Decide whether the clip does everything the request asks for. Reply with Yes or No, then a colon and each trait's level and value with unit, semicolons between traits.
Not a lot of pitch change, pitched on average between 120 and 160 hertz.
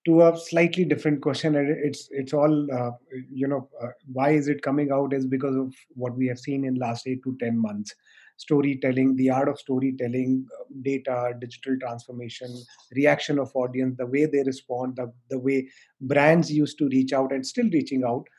Yes: narrow, 2.2 semitones; low, 135 Hz